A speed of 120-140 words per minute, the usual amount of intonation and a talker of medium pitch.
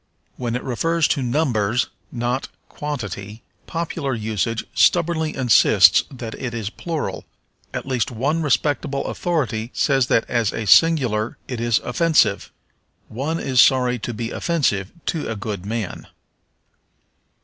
No: slow, 135 wpm; average, 4.9 semitones; low, 125 Hz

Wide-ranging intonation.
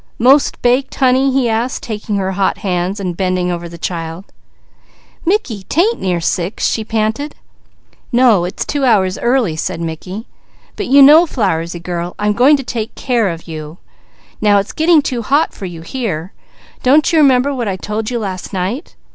Yes: wide, 6.3 semitones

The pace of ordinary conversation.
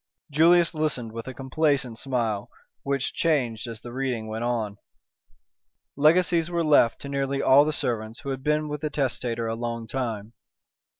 Yes: average, 165 wpm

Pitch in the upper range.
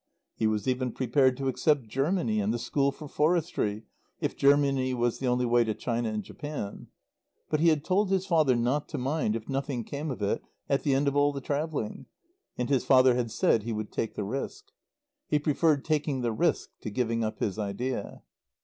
No: low, 130 Hz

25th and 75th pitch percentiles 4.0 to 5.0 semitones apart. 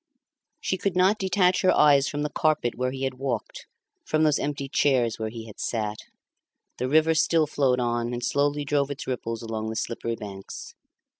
Yes: average, 4.4 semitones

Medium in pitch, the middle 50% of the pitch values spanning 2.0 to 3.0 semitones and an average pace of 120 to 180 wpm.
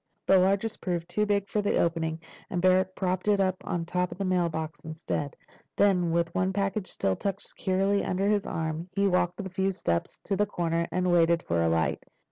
No: medium, 180 Hz; average, 2.7 semitones; average, 200 wpm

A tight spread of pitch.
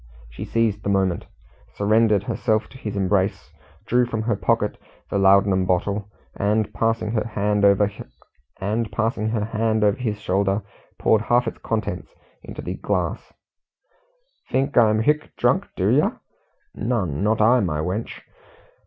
Yes: narrow, 2.3 semitones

